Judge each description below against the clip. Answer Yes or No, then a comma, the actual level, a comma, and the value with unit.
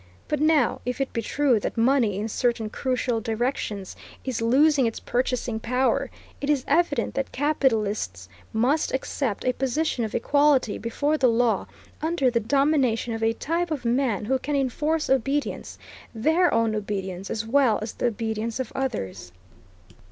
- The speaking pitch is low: No, very high, 250 Hz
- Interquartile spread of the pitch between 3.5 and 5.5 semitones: Yes, average, 4.0 semitones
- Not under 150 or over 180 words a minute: Yes, average, 160 wpm